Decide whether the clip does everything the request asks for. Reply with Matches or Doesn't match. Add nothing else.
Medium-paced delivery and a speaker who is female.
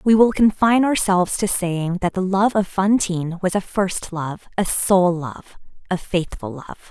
Matches